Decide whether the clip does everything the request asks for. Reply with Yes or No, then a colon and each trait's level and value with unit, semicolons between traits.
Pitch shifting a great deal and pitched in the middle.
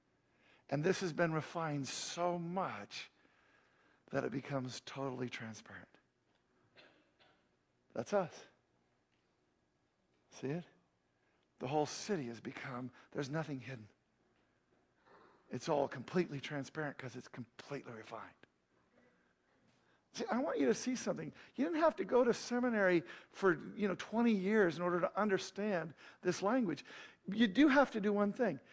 Yes: wide, 7.5 semitones; medium, 160 Hz